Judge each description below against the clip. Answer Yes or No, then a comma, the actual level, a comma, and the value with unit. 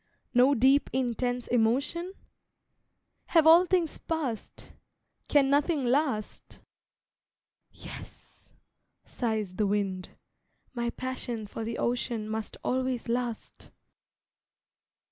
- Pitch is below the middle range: No, high, 245 Hz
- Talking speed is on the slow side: Yes, slow, 90 wpm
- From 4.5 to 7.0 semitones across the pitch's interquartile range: No, average, 3.9 semitones